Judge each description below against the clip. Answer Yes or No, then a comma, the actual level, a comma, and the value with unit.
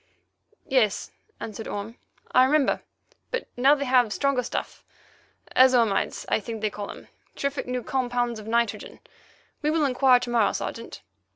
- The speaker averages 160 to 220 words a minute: No, average, 145 wpm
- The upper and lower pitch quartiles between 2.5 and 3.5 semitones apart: Yes, average, 3.0 semitones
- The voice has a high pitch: Yes, high, 245 Hz